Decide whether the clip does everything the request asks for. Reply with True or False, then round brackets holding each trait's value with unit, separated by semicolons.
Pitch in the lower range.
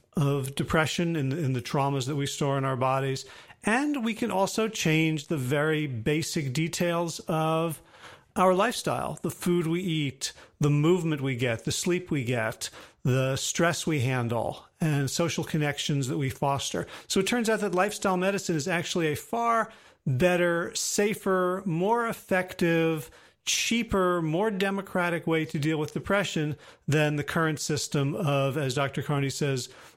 False (160 Hz)